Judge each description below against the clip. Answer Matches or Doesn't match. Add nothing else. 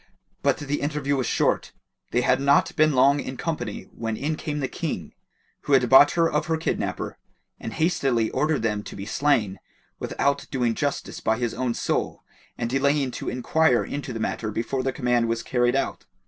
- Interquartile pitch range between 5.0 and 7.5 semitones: Doesn't match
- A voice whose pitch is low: Matches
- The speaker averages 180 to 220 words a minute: Matches